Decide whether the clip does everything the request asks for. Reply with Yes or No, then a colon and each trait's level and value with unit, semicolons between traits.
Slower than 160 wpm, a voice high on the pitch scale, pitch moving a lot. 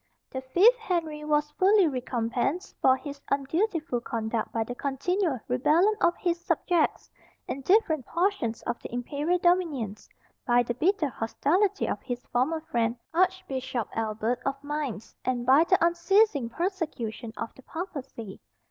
Yes: average, 140 wpm; very high, 285 Hz; wide, 6.3 semitones